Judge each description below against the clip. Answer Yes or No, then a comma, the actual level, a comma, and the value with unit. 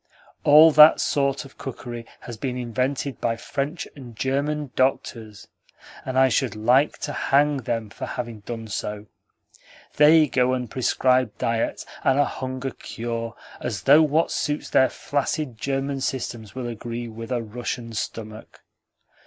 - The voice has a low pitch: Yes, low, 125 Hz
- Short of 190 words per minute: Yes, average, 145 wpm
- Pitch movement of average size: Yes, average, 3.2 semitones